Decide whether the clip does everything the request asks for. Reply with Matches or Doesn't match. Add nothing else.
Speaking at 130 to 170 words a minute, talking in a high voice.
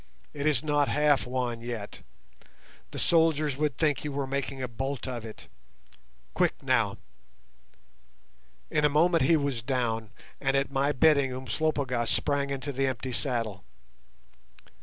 Doesn't match